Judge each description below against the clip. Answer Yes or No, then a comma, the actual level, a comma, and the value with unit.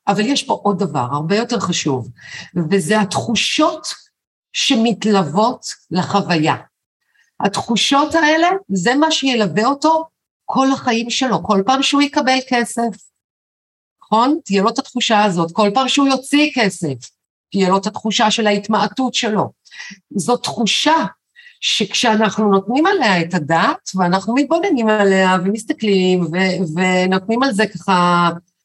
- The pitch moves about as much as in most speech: No, wide, 5.7 semitones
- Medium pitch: No, high, 215 Hz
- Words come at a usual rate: Yes, average, 125 wpm